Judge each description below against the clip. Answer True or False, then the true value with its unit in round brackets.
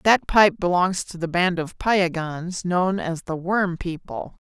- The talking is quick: False (175 wpm)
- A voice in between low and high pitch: True (180 Hz)